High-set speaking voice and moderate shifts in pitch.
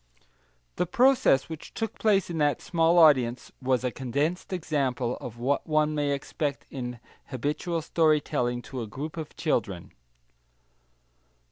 No: medium, 145 Hz; average, 4.3 semitones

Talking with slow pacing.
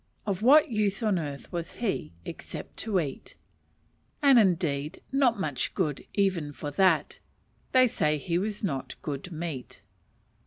No: average, 145 wpm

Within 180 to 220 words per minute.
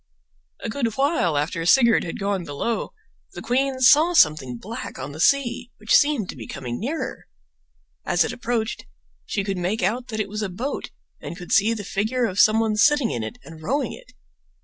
Yes: average, 195 wpm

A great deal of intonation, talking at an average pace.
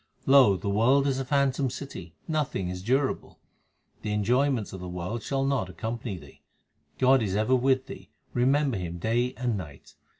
Yes: wide, 5.8 semitones; average, 170 wpm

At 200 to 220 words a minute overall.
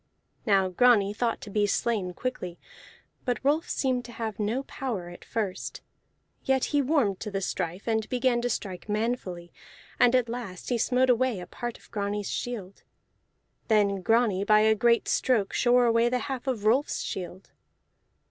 No: average, 165 wpm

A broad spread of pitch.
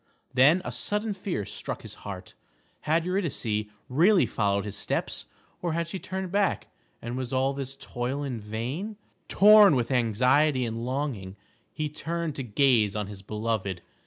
Yes: wide, 7.4 semitones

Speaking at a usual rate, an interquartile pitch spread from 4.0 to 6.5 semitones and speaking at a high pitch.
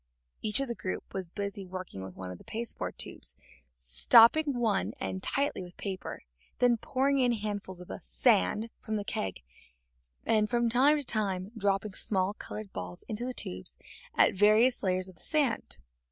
Yes: average, 180 wpm; average, 4.6 semitones; high, 205 Hz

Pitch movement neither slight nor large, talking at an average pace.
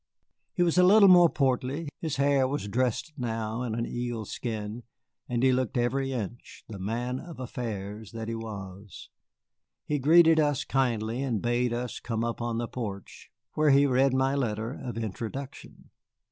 Yes: average, 3.4 semitones; average, 165 wpm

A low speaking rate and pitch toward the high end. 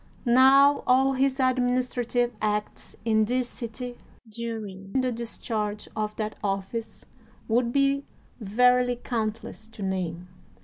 Yes: slow, 115 wpm; high, 235 Hz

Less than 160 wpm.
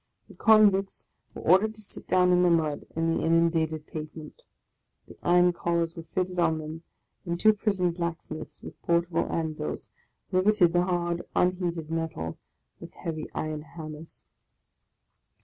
Yes: average, 150 wpm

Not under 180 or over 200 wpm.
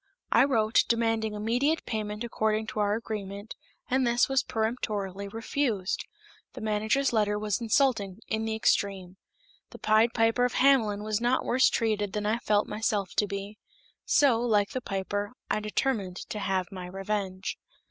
No: average, 155 wpm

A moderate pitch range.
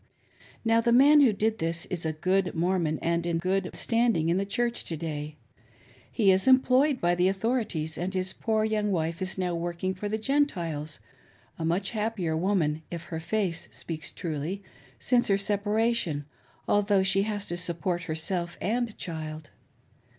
Yes: average, 4.5 semitones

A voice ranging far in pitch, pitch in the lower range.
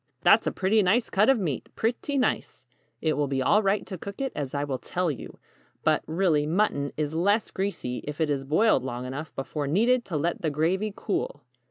No: wide, 6.3 semitones; medium, 165 Hz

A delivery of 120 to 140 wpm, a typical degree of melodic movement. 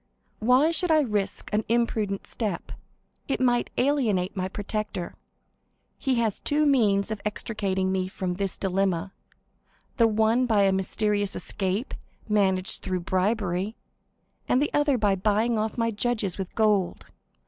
Yes: slow, 135 wpm; average, 3.5 semitones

